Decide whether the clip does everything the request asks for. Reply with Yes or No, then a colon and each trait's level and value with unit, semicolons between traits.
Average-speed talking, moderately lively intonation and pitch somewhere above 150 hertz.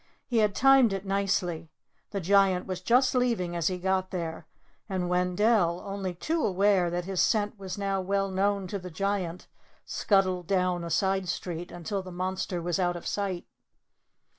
No: average, 175 wpm; narrow, 2.0 semitones; high, 190 Hz